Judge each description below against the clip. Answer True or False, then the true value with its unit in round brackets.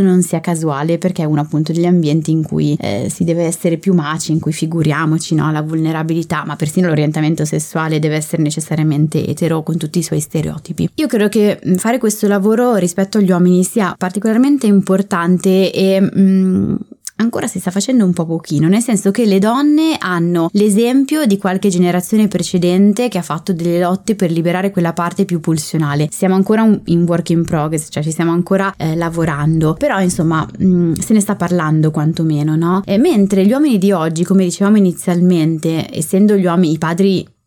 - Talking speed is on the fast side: True (185 wpm)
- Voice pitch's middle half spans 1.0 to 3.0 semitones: False (3.5 semitones)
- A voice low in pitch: False (175 Hz)